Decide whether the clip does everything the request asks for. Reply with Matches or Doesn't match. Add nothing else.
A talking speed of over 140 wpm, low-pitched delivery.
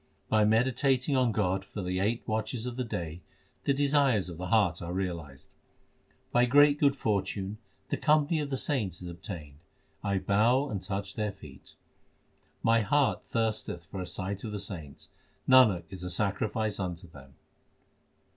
Matches